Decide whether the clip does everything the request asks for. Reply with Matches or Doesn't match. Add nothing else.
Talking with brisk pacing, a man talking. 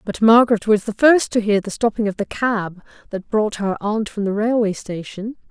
Doesn't match